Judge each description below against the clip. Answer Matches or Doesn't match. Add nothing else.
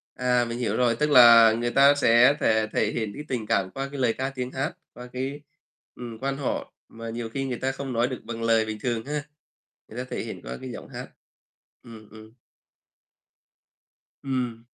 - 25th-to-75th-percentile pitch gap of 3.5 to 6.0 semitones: Doesn't match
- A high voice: Doesn't match